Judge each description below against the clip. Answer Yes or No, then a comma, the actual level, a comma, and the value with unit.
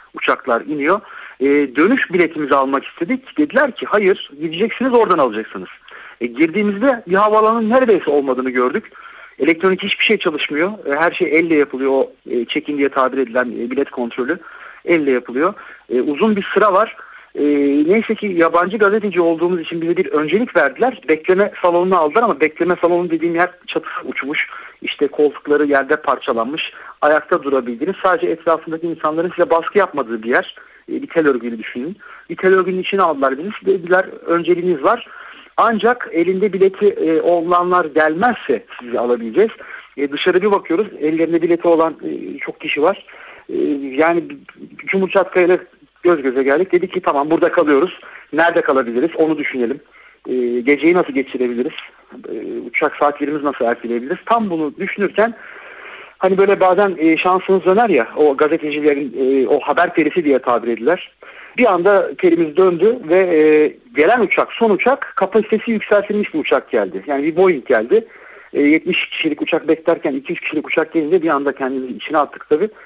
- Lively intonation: Yes, wide, 5.9 semitones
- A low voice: No, medium, 170 Hz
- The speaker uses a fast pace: Yes, fast, 155 wpm